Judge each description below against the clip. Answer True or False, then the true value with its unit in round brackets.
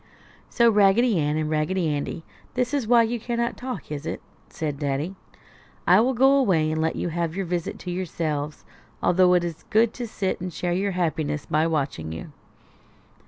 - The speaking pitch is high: False (175 Hz)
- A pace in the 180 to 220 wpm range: True (185 wpm)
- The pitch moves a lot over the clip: True (6.1 semitones)